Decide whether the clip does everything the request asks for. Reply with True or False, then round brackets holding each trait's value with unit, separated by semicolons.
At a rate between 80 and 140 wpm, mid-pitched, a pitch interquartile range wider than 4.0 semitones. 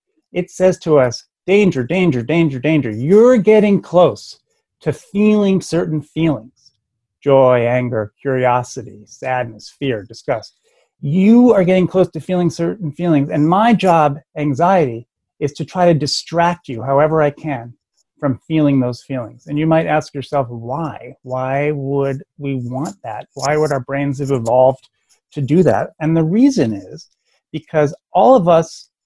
False (155 wpm; 150 Hz; 5.0 semitones)